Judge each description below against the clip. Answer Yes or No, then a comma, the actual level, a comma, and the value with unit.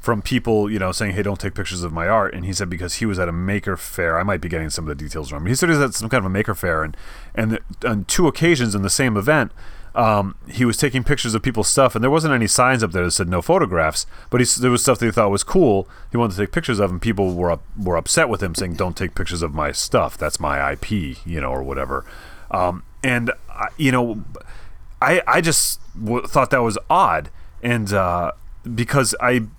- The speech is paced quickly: Yes, fast, 255 wpm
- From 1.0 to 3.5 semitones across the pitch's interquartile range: No, average, 5.2 semitones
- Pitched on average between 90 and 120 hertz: Yes, low, 100 Hz